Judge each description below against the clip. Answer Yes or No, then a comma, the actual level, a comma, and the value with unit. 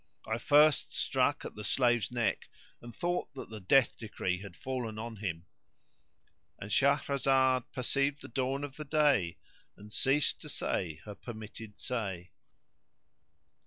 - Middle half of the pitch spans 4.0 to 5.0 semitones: Yes, average, 4.7 semitones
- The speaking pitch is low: Yes, low, 120 Hz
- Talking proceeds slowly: Yes, slow, 130 wpm